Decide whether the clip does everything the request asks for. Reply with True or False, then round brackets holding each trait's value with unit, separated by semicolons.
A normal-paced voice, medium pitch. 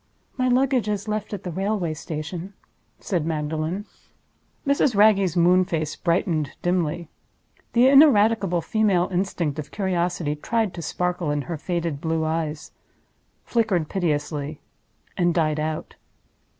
False (120 wpm; 175 Hz)